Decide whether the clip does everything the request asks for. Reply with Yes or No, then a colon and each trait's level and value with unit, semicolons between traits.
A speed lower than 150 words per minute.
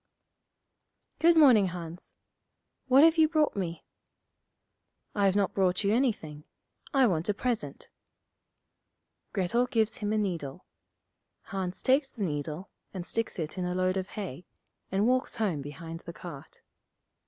Yes: average, 140 wpm